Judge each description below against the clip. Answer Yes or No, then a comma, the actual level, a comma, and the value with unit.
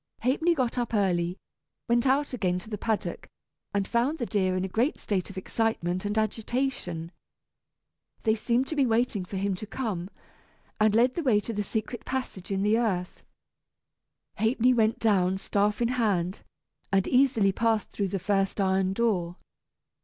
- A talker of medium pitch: No, high, 215 Hz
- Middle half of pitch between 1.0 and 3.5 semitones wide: No, average, 3.9 semitones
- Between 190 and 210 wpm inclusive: No, average, 170 wpm